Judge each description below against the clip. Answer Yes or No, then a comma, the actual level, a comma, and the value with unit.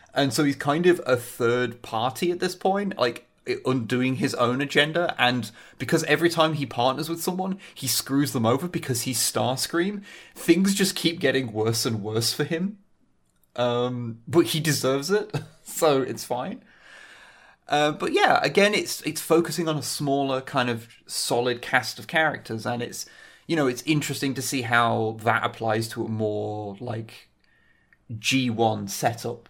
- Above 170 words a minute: No, average, 165 wpm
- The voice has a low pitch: Yes, low, 130 Hz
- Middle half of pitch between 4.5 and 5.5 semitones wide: Yes, average, 5.2 semitones